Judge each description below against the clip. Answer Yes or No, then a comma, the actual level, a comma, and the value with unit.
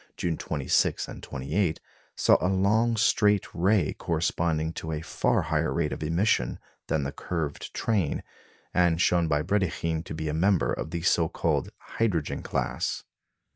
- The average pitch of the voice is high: No, very low, 85 Hz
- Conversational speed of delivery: Yes, average, 155 wpm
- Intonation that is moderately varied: Yes, average, 3.3 semitones